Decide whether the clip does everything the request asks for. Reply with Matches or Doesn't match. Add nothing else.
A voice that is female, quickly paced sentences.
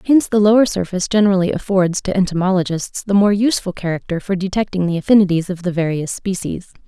Doesn't match